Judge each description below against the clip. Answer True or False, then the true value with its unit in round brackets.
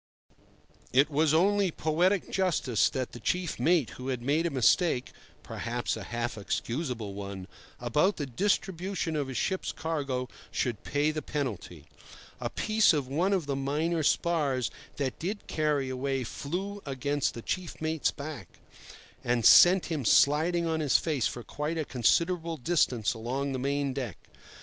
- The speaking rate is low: False (150 wpm)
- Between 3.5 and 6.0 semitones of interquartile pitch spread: True (4.7 semitones)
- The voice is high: False (145 Hz)